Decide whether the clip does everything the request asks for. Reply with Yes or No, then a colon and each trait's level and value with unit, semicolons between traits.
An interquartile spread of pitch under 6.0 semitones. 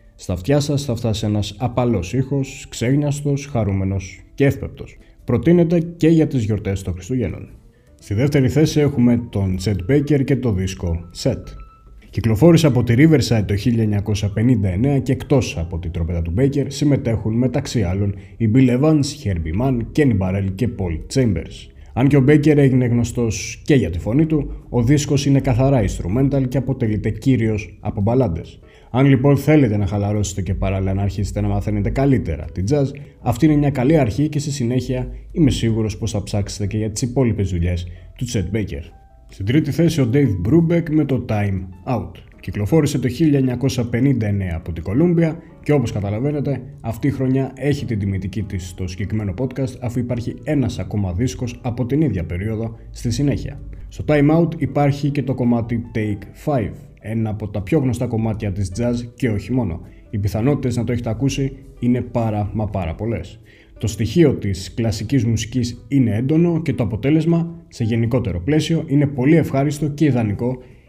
Yes: average, 5.3 semitones